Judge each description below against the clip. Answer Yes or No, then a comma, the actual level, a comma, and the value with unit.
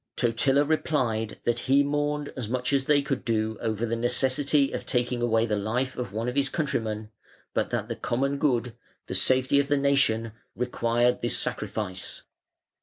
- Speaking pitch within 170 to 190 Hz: No, low, 125 Hz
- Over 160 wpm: Yes, average, 175 wpm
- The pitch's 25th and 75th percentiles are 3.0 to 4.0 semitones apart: Yes, average, 3.5 semitones